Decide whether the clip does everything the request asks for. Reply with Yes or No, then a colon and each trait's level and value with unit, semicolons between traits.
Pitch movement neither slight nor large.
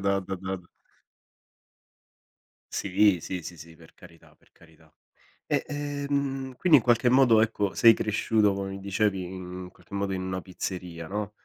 Yes: average, 3.7 semitones